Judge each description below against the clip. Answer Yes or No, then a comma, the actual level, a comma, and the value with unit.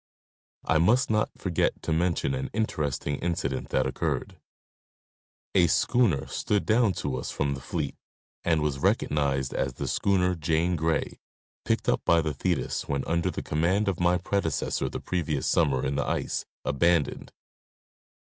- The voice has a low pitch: Yes, very low, 80 Hz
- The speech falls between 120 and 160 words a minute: Yes, average, 150 wpm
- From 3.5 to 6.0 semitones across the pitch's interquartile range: Yes, average, 4.3 semitones